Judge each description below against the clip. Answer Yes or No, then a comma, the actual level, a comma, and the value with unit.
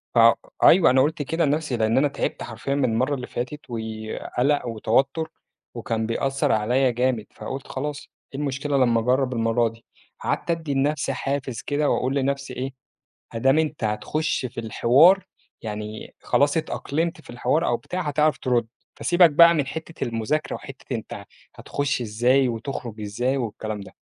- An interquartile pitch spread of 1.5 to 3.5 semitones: No, average, 4.1 semitones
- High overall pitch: No, low, 130 Hz